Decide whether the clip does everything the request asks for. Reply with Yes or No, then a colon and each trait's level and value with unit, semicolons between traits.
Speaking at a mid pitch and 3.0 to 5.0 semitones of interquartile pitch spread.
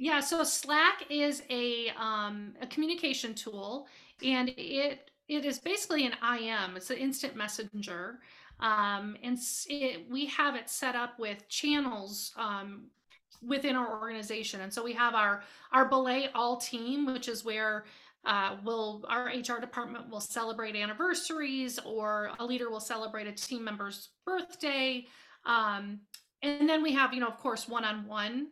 No: high, 240 Hz; average, 4.3 semitones